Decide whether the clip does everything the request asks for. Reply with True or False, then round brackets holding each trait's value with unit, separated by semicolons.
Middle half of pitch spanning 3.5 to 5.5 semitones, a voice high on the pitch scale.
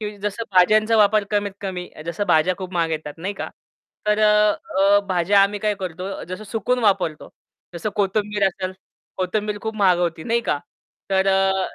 False (2.4 semitones; 195 Hz)